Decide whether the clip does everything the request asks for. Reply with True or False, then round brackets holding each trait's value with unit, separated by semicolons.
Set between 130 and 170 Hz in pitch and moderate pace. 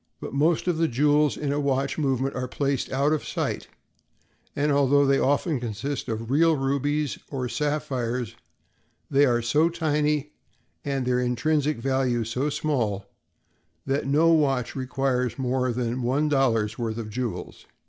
True (135 Hz; 150 wpm)